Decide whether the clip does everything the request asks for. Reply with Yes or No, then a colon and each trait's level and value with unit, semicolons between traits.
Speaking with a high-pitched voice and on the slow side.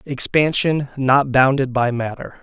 No: low, 135 Hz; slow, 125 wpm